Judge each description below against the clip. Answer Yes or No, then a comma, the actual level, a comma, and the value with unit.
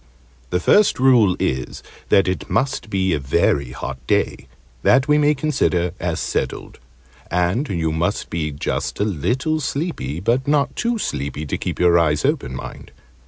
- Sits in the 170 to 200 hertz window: No, very low, 90 Hz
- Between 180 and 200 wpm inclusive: No, average, 165 wpm